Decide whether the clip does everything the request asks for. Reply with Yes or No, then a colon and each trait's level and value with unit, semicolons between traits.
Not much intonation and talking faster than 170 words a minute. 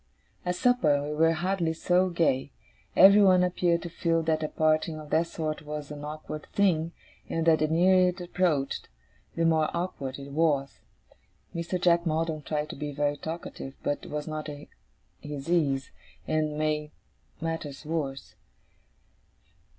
No: narrow, 2.3 semitones; average, 150 wpm